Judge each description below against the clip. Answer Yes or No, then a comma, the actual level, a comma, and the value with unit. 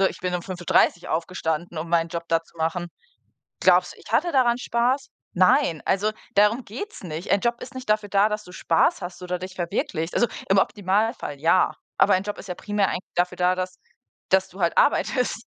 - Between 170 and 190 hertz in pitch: Yes, medium, 185 Hz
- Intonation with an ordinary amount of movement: Yes, average, 3.5 semitones